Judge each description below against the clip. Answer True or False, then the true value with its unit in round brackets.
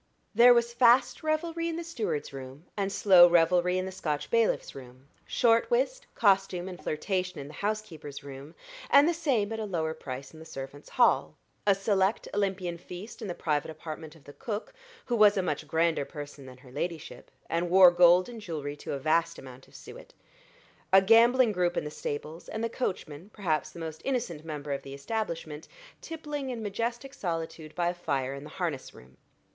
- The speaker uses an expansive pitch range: True (6.5 semitones)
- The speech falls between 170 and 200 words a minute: True (195 wpm)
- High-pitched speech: False (175 Hz)